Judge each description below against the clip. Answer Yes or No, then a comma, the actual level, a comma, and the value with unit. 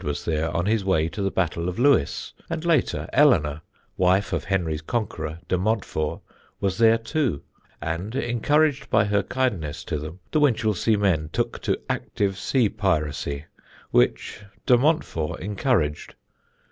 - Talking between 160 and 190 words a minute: No, average, 145 wpm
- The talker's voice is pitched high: No, very low, 95 Hz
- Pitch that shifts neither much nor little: No, wide, 6.4 semitones